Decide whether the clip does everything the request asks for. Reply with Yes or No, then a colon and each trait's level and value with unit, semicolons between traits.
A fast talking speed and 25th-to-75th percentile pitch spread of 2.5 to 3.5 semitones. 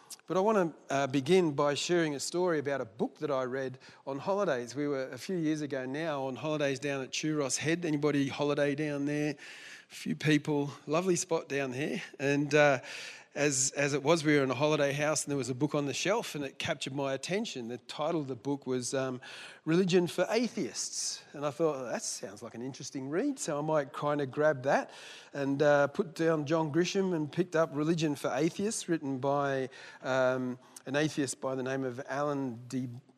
Yes: fast, 210 wpm; average, 3.0 semitones